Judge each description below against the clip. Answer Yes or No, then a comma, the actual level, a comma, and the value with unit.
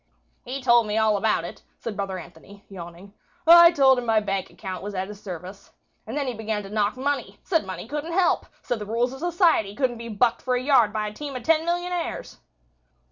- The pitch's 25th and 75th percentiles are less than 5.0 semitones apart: No, wide, 5.5 semitones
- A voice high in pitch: Yes, high, 230 Hz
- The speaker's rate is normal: No, fast, 220 wpm